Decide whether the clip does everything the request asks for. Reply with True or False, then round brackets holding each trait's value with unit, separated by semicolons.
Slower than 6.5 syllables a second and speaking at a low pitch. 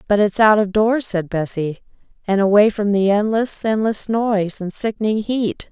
False (4.7 syllables/s; 210 Hz)